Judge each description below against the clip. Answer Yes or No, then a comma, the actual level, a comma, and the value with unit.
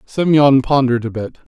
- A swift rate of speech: No, average, 155 wpm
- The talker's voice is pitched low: Yes, low, 130 Hz